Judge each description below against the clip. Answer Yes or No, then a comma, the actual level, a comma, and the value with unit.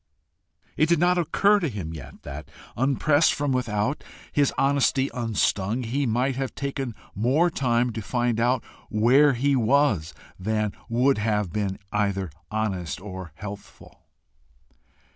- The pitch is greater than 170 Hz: No, low, 120 Hz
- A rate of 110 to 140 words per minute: Yes, slow, 135 wpm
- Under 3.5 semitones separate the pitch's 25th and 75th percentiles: No, average, 4.9 semitones